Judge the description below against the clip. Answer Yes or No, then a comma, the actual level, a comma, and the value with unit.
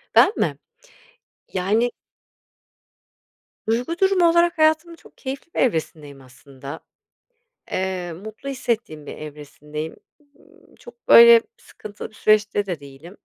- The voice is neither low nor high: No, high, 215 Hz